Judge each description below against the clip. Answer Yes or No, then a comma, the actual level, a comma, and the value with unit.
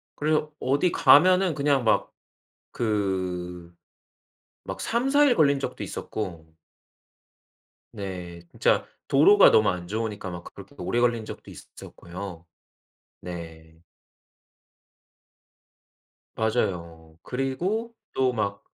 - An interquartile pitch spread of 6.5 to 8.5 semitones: Yes, wide, 8.2 semitones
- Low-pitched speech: Yes, low, 110 Hz